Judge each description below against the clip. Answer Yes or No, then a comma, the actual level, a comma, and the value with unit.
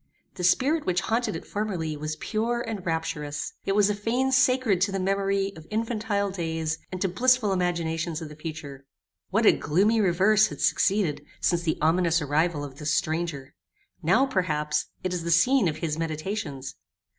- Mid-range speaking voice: Yes, medium, 180 Hz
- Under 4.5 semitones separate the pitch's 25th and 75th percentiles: No, average, 4.9 semitones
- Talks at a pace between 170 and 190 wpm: Yes, average, 175 wpm